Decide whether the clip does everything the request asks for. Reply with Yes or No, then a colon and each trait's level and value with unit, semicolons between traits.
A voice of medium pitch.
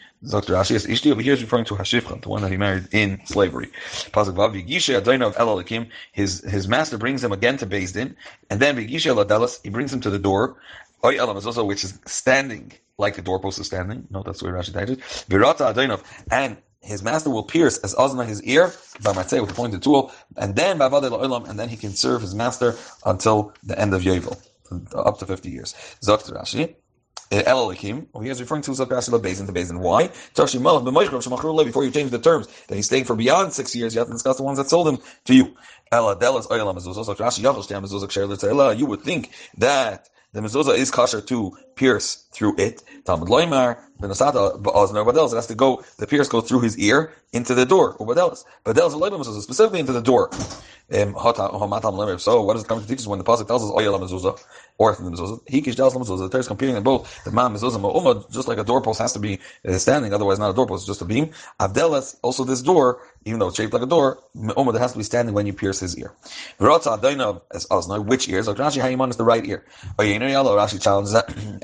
No: low, 115 Hz